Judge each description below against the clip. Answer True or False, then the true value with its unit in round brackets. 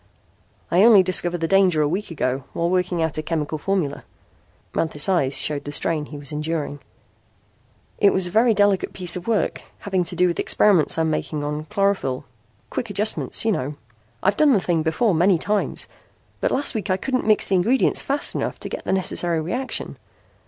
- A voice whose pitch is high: False (180 Hz)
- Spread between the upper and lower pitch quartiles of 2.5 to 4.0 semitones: False (4.4 semitones)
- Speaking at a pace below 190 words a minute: False (195 wpm)